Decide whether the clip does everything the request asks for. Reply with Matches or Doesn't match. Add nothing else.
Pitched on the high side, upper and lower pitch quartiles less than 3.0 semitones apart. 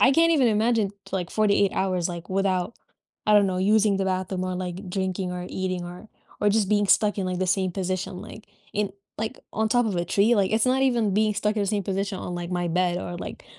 Matches